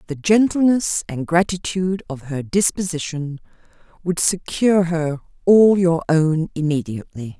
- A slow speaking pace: Yes, slow, 115 wpm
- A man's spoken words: No, female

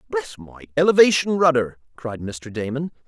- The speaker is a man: Yes, male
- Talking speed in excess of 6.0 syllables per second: No, 5.0 syllables/s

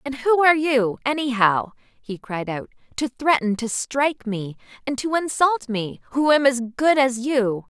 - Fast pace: No, average, 175 wpm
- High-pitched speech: Yes, very high, 250 Hz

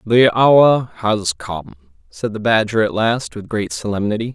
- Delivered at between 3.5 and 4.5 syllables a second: Yes, 4.1 syllables/s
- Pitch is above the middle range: No, low, 105 Hz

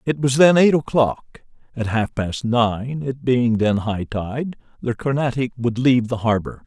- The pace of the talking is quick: No, average, 180 wpm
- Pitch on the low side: Yes, low, 125 Hz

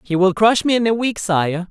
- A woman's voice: No, male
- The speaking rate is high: Yes, fast, 280 wpm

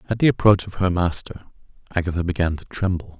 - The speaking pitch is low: Yes, very low, 90 Hz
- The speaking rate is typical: Yes, average, 190 wpm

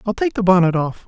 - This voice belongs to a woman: No, male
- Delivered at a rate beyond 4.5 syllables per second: Yes, 6.3 syllables/s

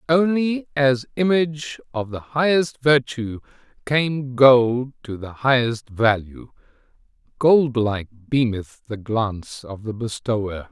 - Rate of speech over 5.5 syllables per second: No, 3.9 syllables/s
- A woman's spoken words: No, male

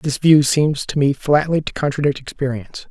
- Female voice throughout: No, male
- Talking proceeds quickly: No, average, 185 wpm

